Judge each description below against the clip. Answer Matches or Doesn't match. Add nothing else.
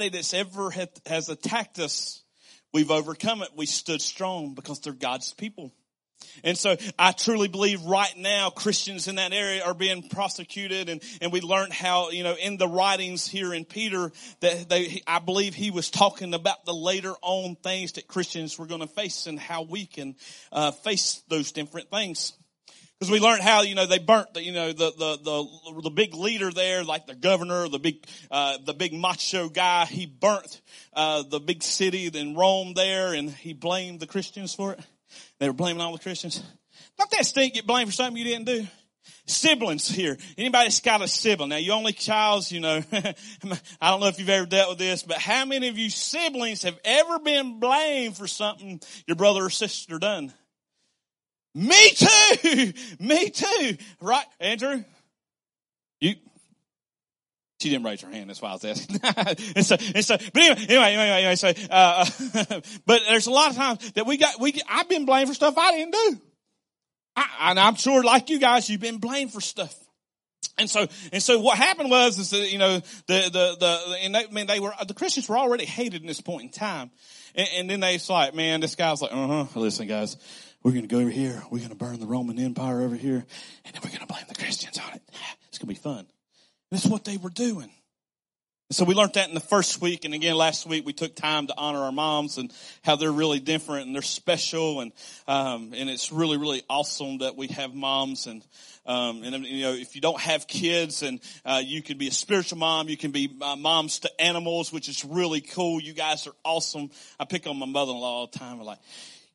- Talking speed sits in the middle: Doesn't match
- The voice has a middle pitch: Matches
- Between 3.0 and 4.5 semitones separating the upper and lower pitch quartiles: Doesn't match